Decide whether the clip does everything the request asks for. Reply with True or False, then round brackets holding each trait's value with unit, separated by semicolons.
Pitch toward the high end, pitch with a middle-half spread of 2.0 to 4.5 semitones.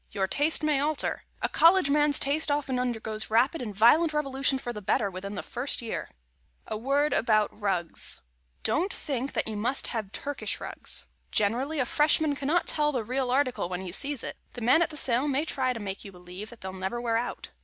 False (255 Hz; 5.2 semitones)